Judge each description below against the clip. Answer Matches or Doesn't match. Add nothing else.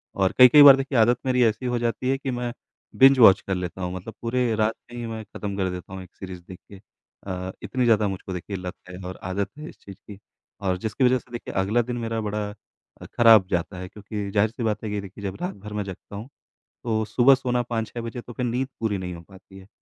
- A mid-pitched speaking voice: Doesn't match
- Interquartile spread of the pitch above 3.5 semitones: Matches